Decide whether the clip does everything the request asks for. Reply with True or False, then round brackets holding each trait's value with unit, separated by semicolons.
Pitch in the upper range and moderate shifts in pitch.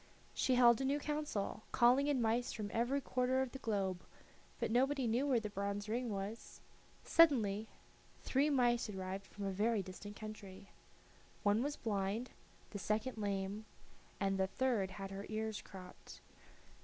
True (220 Hz; 4.2 semitones)